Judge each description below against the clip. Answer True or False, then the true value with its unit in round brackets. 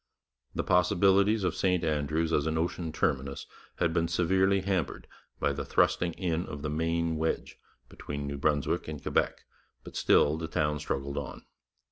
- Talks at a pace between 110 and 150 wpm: False (160 wpm)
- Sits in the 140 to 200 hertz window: False (80 Hz)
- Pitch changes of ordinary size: True (3.2 semitones)